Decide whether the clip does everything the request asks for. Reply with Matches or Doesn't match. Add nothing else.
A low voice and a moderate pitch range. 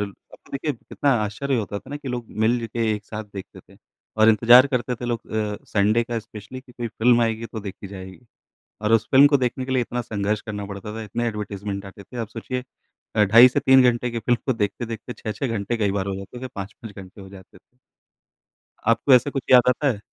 Matches